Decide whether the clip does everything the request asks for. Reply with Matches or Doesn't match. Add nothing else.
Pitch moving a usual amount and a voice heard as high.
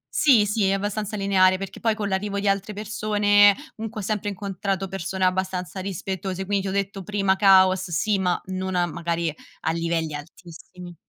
Doesn't match